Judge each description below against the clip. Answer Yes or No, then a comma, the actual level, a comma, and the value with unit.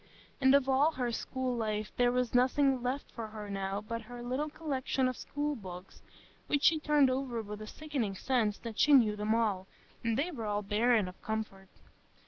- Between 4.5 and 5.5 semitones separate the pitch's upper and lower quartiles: No, average, 4.1 semitones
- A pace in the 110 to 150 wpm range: No, average, 190 wpm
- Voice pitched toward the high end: Yes, high, 240 Hz